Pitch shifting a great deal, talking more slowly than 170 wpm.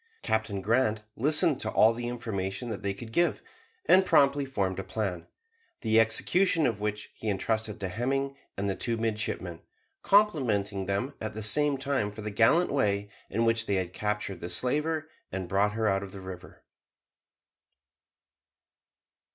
No: average, 4.8 semitones; average, 160 wpm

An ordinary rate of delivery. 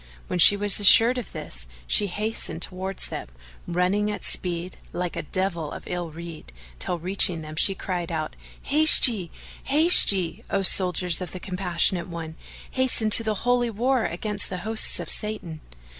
Yes: average, 170 wpm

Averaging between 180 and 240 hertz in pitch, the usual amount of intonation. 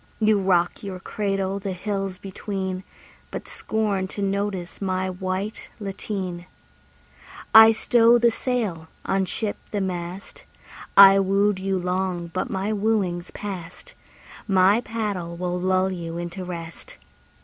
No: high, 190 Hz; narrow, 2.0 semitones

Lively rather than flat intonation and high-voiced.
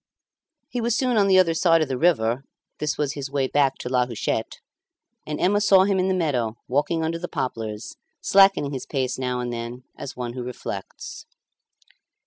No: wide, 6.3 semitones; medium, 140 Hz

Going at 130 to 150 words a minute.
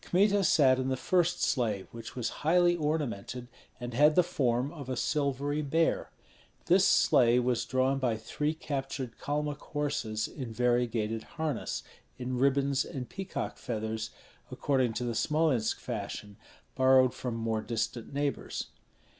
Yes: average, 140 wpm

